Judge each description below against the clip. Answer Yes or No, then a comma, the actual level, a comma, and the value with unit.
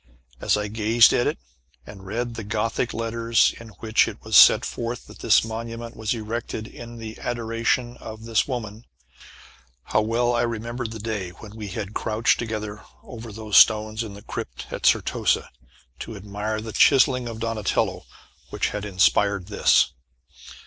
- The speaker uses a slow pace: No, average, 160 wpm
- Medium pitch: No, low, 110 Hz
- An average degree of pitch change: No, narrow, 1.6 semitones